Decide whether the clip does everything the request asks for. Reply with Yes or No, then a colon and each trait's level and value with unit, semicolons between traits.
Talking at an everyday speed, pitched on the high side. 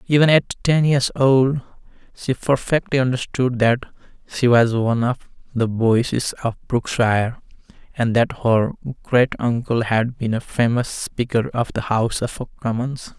No: average, 145 wpm; low, 125 Hz